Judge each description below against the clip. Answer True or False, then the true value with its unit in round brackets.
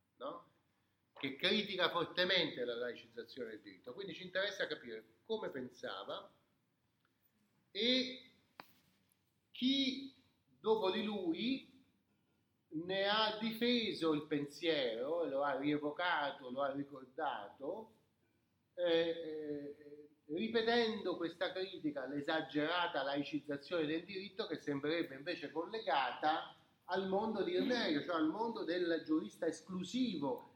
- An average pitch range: False (6.8 semitones)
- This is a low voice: False (175 Hz)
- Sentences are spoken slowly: True (100 wpm)